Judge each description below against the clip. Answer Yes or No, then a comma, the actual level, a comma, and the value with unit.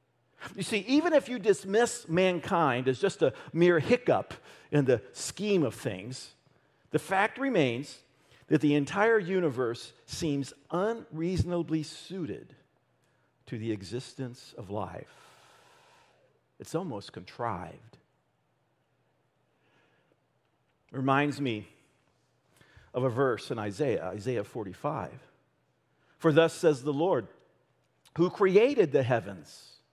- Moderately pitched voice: Yes, medium, 155 Hz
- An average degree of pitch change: No, wide, 6.2 semitones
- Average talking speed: No, slow, 110 wpm